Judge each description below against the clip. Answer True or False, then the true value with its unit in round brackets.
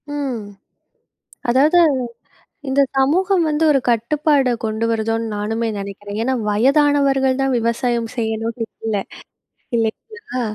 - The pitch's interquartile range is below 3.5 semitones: False (4.1 semitones)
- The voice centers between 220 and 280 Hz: True (250 Hz)